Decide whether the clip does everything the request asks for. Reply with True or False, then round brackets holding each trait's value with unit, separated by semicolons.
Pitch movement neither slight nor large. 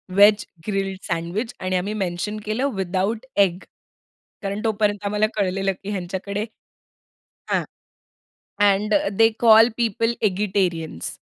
False (2.2 semitones)